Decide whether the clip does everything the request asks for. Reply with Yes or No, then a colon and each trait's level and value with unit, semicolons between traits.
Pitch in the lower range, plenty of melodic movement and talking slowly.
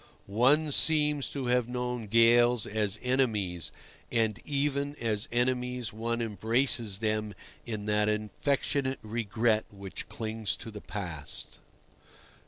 No: low, 115 Hz; average, 2.9 semitones; slow, 115 wpm